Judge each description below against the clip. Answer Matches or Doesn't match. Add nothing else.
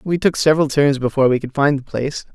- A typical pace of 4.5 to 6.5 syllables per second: Doesn't match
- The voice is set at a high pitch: Doesn't match